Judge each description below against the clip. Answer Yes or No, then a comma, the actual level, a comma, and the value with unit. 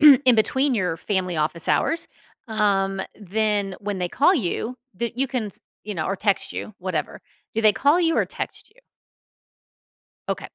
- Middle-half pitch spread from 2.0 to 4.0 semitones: No, average, 4.9 semitones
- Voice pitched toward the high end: Yes, high, 210 Hz